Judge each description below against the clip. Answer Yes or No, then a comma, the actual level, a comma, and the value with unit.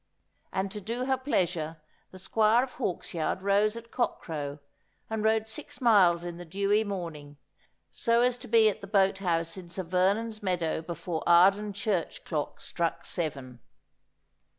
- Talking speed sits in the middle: Yes, average, 155 wpm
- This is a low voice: No, high, 190 Hz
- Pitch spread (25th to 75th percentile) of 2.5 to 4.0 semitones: No, average, 4.4 semitones